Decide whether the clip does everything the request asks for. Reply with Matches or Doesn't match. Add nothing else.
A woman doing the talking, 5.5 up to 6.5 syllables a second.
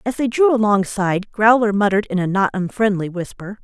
Matches